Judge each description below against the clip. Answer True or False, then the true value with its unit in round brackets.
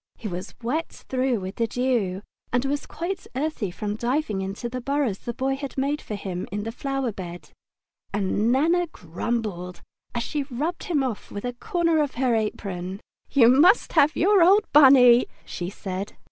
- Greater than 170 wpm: True (180 wpm)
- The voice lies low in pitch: False (245 Hz)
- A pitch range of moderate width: False (5.9 semitones)